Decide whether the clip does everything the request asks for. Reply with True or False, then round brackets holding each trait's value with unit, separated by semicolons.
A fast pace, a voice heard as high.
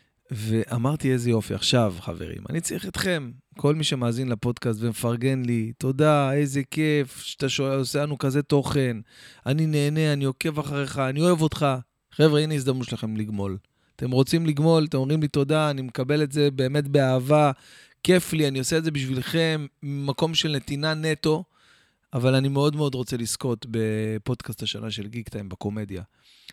False (160 wpm; 135 Hz)